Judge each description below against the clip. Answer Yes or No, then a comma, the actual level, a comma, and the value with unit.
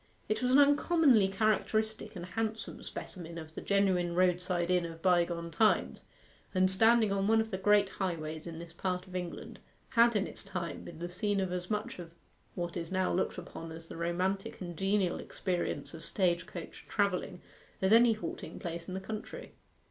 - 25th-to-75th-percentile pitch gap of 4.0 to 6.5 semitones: No, average, 3.3 semitones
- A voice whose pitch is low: No, medium, 185 Hz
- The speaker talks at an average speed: Yes, average, 185 wpm